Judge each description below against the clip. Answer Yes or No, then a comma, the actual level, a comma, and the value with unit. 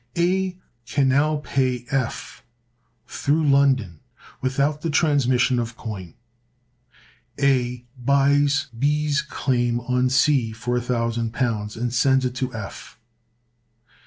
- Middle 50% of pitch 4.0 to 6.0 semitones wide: No, average, 2.9 semitones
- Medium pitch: No, low, 130 Hz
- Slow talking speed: Yes, slow, 105 wpm